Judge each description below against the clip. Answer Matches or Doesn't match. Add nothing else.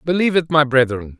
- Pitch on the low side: Doesn't match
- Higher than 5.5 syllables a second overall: Matches